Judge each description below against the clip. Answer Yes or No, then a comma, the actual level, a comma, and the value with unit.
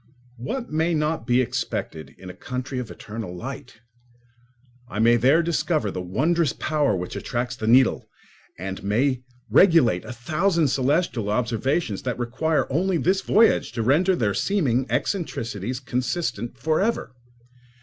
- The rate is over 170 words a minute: No, average, 140 wpm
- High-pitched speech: No, low, 130 Hz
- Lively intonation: Yes, wide, 5.8 semitones